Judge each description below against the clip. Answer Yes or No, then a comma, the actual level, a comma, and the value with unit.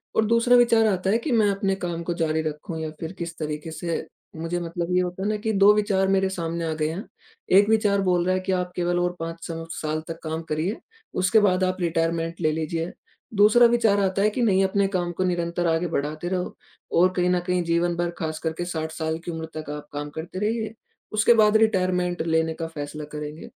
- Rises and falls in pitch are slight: No, average, 3.2 semitones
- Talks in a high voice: No, medium, 175 Hz